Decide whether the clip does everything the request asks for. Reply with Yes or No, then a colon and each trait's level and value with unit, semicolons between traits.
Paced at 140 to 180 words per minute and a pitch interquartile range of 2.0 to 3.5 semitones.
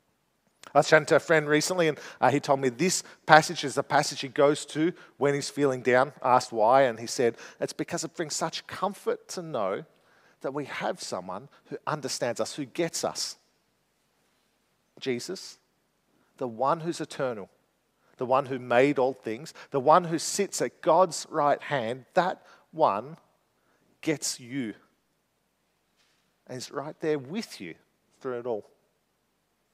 No: average, 155 wpm; average, 3.9 semitones